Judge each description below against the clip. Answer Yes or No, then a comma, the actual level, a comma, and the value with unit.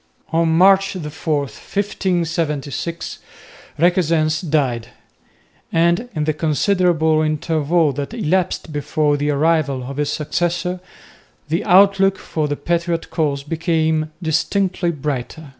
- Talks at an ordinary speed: No, slow, 110 wpm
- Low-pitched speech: No, medium, 160 Hz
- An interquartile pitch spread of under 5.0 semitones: Yes, average, 2.7 semitones